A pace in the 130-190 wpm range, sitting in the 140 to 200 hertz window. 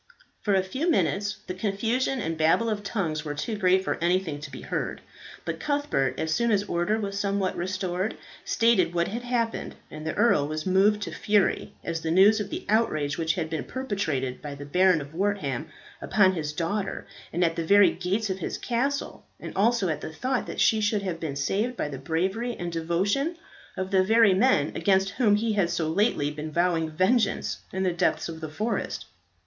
No: average, 200 wpm; high, 190 Hz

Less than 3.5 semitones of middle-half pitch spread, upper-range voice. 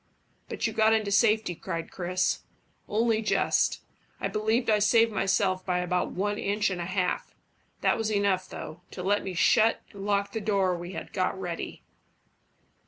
Yes: average, 2.8 semitones; high, 200 Hz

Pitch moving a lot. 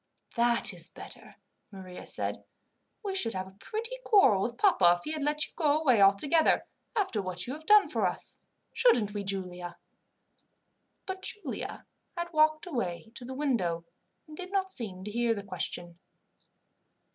Yes: wide, 8.9 semitones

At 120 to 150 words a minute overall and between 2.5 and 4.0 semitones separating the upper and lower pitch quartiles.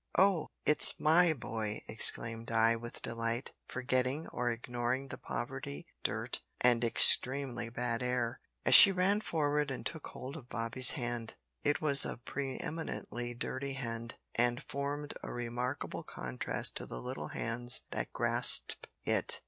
Yes: average, 145 wpm; average, 3.4 semitones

